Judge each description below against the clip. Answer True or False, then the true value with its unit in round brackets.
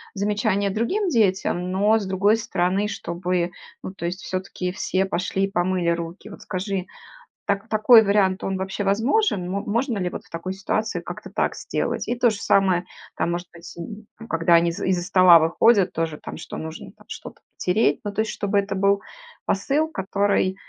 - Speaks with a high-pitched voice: True (195 Hz)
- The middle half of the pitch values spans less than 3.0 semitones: True (2.4 semitones)